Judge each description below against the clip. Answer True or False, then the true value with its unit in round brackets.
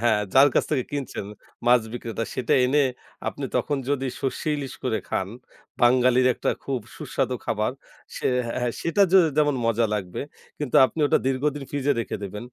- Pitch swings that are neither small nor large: True (3.5 semitones)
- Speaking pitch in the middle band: False (130 Hz)